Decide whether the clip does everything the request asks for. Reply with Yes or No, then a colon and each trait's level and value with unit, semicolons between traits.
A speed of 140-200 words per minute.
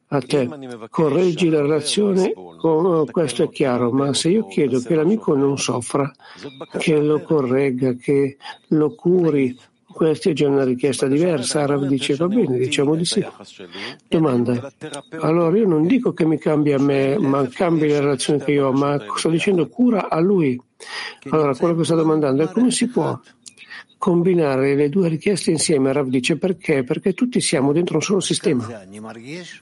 Yes: fast, 170 wpm